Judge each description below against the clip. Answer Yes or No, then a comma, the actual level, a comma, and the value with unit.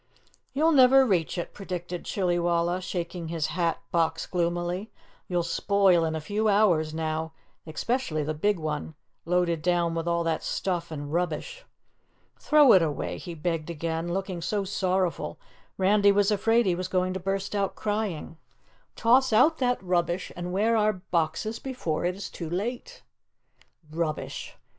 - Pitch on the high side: No, medium, 180 Hz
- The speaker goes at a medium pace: Yes, average, 155 wpm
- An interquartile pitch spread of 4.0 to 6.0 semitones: No, average, 3.5 semitones